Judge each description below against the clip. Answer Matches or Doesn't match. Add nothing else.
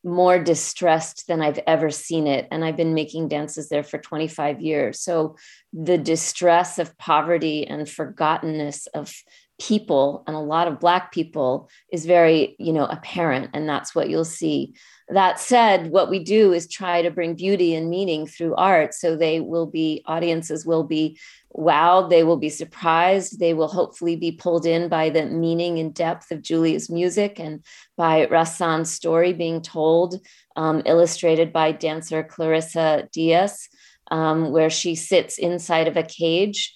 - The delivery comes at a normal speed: Matches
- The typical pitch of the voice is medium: Matches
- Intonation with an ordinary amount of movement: Doesn't match